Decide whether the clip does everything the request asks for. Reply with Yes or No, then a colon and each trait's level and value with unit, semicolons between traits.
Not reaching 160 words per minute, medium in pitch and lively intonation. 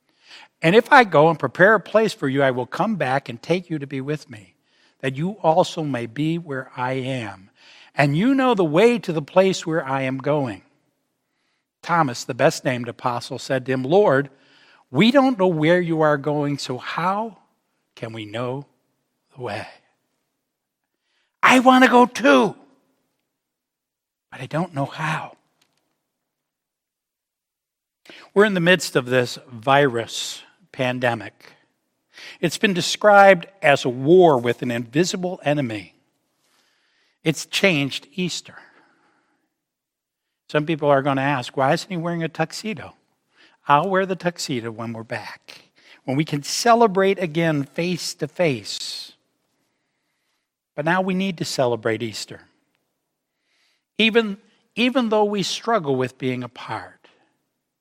Yes: average, 140 wpm; medium, 150 Hz; wide, 6.1 semitones